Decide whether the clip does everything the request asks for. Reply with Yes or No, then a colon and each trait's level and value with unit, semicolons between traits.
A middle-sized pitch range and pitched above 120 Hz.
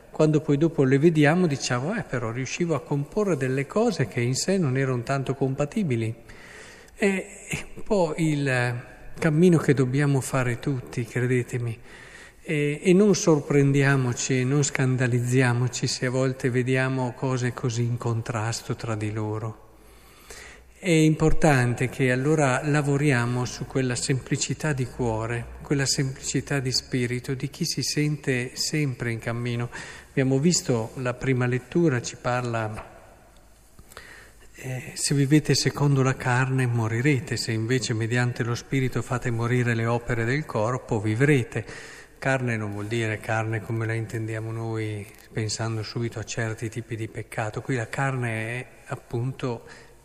Yes: average, 3.3 semitones; low, 130 Hz